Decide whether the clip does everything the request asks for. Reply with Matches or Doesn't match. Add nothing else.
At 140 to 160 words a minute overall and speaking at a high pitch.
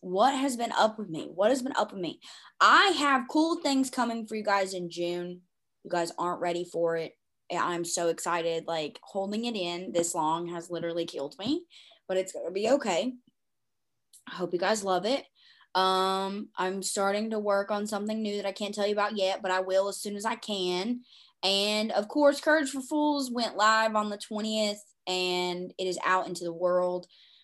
Doesn't match